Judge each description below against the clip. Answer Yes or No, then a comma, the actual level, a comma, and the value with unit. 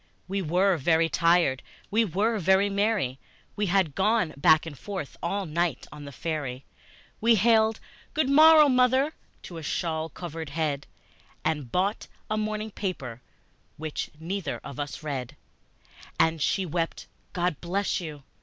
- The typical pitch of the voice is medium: Yes, medium, 175 Hz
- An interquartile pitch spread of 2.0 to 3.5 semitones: No, average, 4.9 semitones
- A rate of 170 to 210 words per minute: No, average, 145 wpm